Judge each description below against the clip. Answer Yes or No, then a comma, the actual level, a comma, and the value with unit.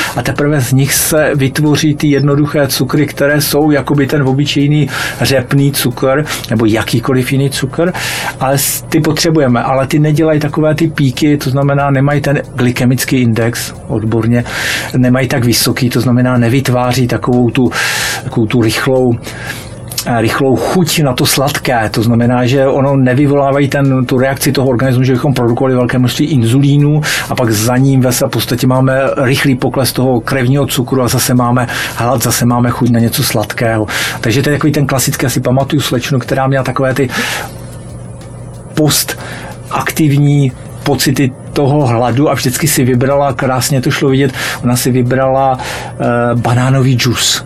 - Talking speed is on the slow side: No, average, 155 wpm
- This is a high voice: No, low, 130 Hz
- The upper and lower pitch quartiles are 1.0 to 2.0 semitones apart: No, narrow, 2.4 semitones